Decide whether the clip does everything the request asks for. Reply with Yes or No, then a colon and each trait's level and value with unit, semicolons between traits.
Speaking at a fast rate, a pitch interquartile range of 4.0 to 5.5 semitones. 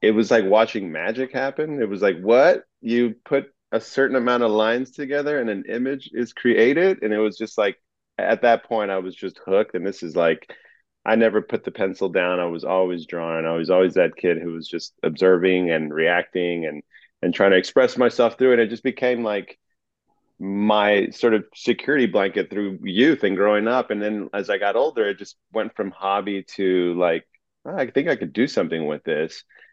Yes: fast, 210 wpm; average, 4.7 semitones